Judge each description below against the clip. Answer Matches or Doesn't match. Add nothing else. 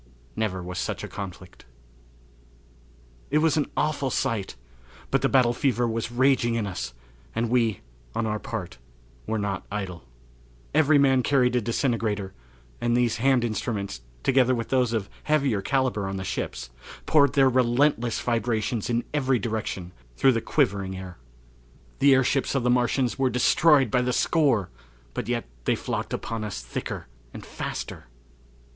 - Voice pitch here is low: Matches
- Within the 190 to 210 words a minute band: Doesn't match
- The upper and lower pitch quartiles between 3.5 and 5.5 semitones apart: Matches